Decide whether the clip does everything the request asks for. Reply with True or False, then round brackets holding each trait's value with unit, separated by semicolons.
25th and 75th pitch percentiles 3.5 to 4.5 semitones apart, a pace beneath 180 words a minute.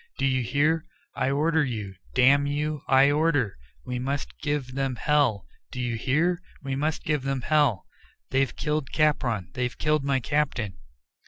False (3.1 semitones; 160 wpm)